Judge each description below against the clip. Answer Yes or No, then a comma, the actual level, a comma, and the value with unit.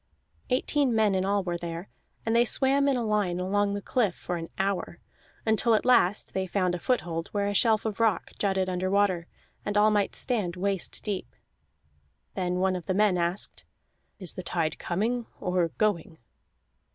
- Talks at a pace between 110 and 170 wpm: No, average, 180 wpm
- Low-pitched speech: No, high, 200 Hz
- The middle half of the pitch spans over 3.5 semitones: No, average, 3.1 semitones